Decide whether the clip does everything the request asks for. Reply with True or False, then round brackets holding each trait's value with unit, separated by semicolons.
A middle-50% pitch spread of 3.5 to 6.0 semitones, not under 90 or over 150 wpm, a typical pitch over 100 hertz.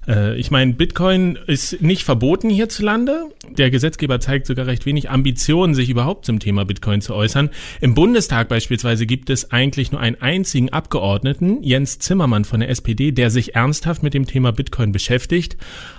False (4.5 semitones; 165 wpm; 135 Hz)